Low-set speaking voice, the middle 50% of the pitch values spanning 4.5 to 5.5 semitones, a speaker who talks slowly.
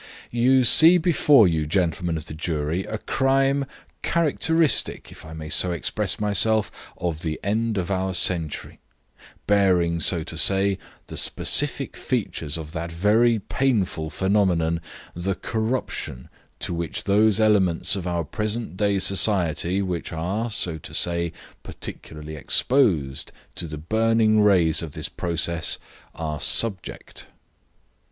Yes: very low, 95 Hz; average, 4.9 semitones; slow, 130 wpm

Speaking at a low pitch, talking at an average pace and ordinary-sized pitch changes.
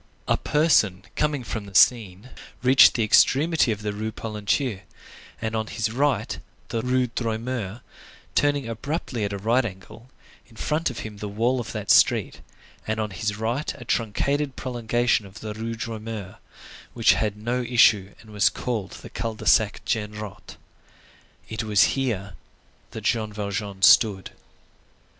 Yes: low, 110 Hz; average, 160 wpm; average, 3.0 semitones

